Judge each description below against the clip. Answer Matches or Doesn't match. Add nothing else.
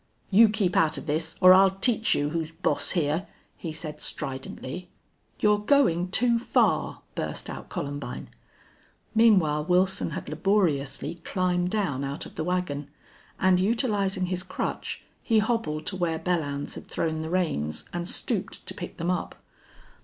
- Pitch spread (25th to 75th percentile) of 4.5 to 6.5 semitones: Doesn't match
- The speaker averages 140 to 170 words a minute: Matches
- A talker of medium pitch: Matches